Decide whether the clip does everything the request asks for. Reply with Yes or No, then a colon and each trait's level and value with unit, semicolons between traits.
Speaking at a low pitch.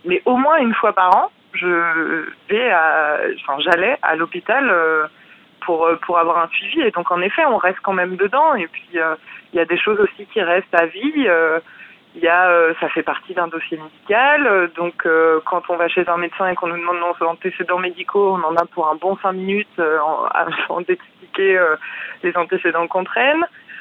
No: medium, 180 Hz